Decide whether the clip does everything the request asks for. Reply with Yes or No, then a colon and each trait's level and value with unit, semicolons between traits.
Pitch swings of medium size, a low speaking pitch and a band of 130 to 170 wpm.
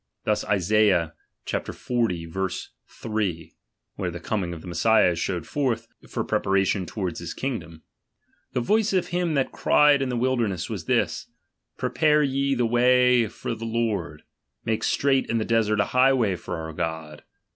No: wide, 6.2 semitones; low, 110 Hz; average, 160 wpm